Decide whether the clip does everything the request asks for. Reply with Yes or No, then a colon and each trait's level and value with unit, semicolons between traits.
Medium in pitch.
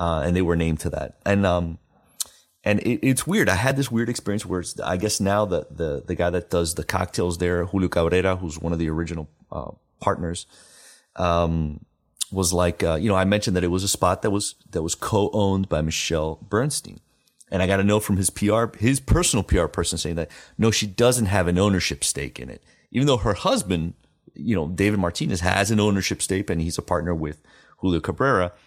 No: very low, 95 Hz